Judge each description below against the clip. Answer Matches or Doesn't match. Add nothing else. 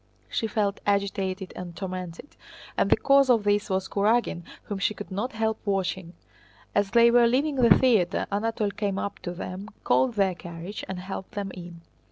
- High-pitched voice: Matches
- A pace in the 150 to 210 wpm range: Matches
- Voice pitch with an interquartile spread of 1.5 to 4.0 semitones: Matches